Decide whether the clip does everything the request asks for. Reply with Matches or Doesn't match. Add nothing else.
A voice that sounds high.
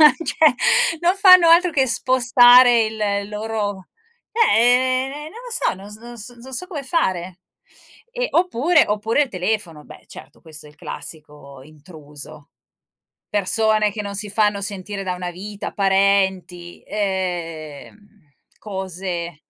Matches